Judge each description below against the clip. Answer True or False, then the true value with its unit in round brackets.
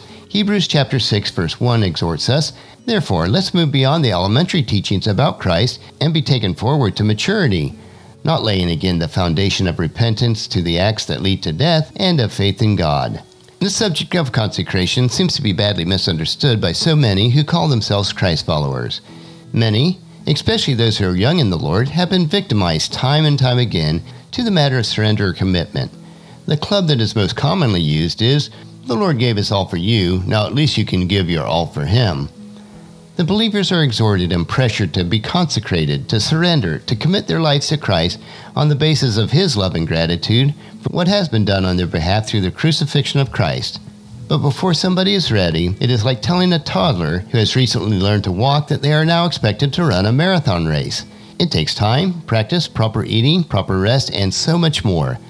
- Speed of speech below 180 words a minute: False (200 wpm)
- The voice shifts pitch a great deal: True (7.8 semitones)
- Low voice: True (120 Hz)